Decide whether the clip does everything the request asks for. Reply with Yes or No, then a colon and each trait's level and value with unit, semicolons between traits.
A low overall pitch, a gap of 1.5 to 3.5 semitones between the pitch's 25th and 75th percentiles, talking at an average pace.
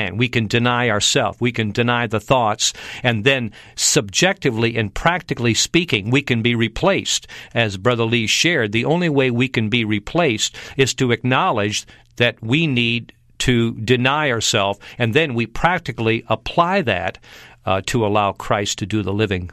Yes: low, 120 Hz; average, 3.1 semitones; average, 165 wpm